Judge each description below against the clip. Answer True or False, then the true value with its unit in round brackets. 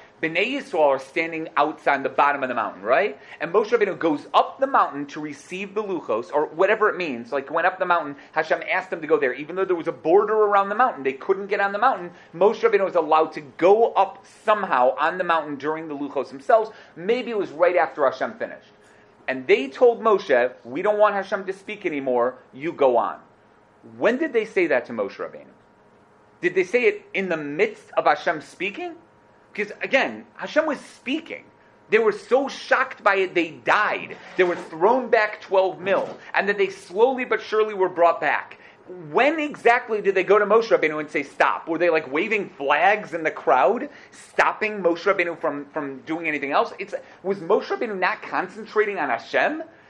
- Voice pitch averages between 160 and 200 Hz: True (190 Hz)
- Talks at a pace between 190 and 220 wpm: True (205 wpm)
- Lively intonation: True (6.7 semitones)